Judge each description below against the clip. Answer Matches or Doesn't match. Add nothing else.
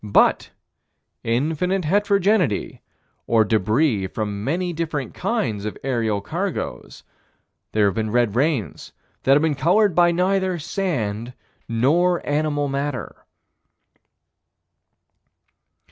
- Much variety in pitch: Matches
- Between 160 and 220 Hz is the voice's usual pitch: Doesn't match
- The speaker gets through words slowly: Matches